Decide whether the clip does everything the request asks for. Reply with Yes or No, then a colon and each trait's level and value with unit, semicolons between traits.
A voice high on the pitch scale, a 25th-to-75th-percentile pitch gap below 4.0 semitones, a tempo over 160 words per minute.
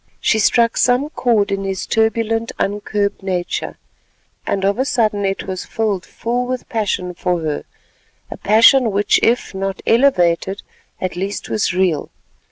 No: high, 205 Hz; average, 3.2 semitones; average, 145 wpm